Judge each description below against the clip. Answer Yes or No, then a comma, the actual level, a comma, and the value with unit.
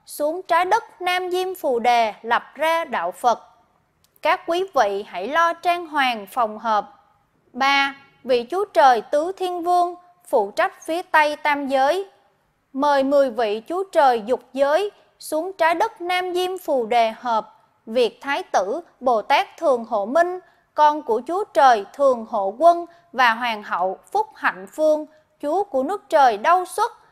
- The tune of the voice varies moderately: No, wide, 6.5 semitones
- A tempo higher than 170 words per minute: No, slow, 165 wpm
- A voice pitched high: Yes, very high, 305 Hz